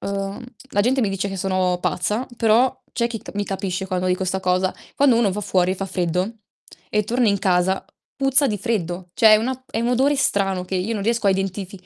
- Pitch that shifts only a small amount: No, average, 3.7 semitones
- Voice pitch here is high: Yes, high, 200 Hz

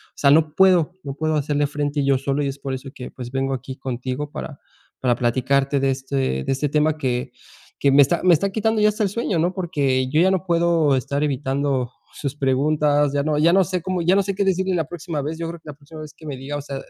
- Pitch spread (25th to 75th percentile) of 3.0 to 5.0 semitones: Yes, average, 3.7 semitones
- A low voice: No, medium, 145 Hz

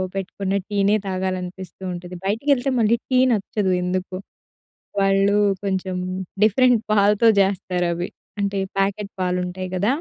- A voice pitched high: Yes, high, 195 Hz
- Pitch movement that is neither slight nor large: No, narrow, 2.1 semitones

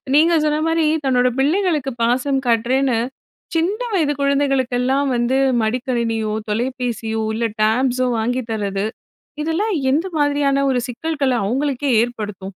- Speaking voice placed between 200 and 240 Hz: No, very high, 260 Hz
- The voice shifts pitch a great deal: No, average, 3.6 semitones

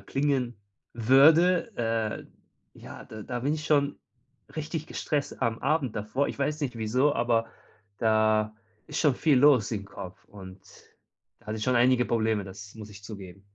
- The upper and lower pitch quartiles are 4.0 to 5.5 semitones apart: Yes, average, 4.8 semitones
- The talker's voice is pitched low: Yes, low, 120 Hz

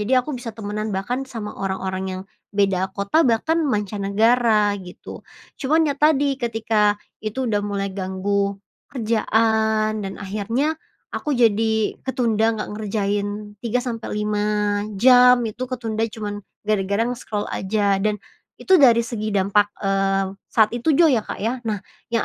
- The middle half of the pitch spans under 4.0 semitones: Yes, narrow, 2.6 semitones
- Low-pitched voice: No, high, 215 Hz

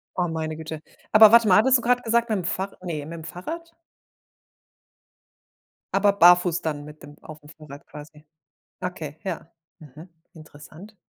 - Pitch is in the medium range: Yes, medium, 170 Hz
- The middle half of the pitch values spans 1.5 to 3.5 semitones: No, average, 4.9 semitones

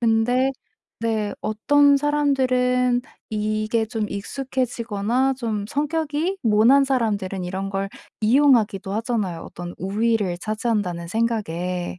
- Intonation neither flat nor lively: Yes, average, 4.2 semitones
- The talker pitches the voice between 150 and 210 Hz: No, high, 225 Hz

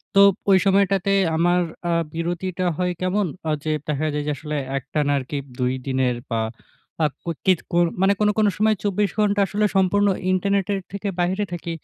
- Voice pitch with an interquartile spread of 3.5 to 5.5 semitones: Yes, average, 4.2 semitones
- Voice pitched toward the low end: No, medium, 185 Hz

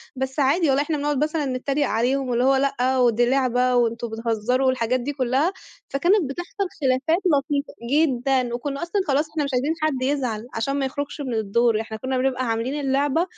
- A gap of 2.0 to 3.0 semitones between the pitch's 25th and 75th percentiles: Yes, average, 2.7 semitones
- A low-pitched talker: No, very high, 265 Hz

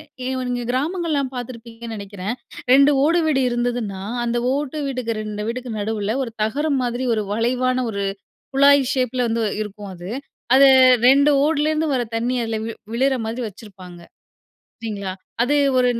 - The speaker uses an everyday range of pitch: Yes, average, 3.5 semitones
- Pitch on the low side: No, high, 245 Hz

